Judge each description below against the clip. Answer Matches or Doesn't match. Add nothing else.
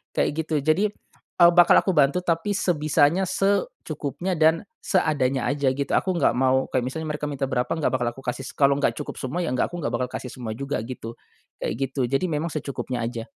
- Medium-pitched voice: Matches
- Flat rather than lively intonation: Doesn't match